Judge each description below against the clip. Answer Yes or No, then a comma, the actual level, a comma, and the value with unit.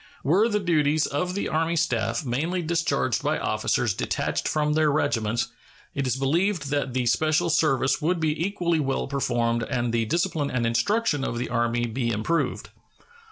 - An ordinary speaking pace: Yes, average, 165 wpm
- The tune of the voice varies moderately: No, wide, 5.7 semitones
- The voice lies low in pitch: No, medium, 145 Hz